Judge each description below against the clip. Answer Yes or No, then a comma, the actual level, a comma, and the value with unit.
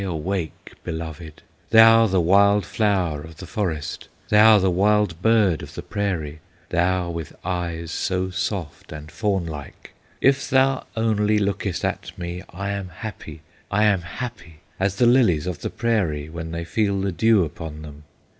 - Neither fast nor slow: Yes, average, 160 wpm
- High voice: No, very low, 95 Hz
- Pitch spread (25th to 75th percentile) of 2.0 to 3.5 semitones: No, average, 4.2 semitones